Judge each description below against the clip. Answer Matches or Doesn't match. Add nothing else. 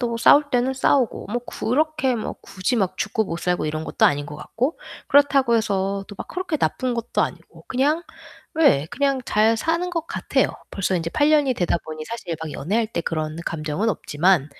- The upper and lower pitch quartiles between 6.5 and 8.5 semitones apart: Matches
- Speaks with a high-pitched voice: Matches